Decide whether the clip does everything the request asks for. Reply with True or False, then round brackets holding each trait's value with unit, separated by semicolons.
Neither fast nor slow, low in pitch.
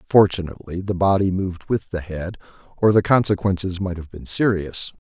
True (165 wpm; 95 Hz)